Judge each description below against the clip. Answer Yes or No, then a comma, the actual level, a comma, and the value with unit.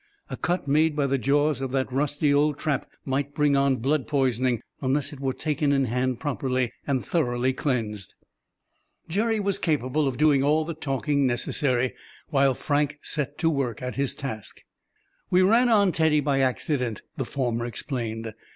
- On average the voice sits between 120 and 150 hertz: Yes, medium, 140 Hz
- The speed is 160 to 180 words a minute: Yes, average, 170 wpm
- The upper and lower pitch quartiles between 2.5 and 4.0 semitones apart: Yes, average, 2.8 semitones